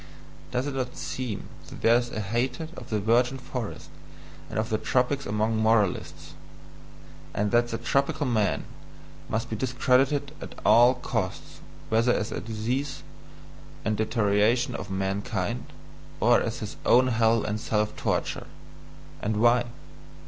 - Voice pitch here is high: No, low, 115 Hz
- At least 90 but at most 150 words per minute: Yes, average, 140 wpm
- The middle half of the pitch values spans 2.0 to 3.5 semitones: Yes, average, 2.7 semitones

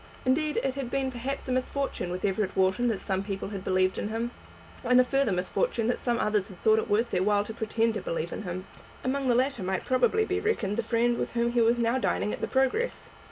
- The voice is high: Yes, high, 235 Hz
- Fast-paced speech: Yes, fast, 245 wpm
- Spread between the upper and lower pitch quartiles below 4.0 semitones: No, average, 4.5 semitones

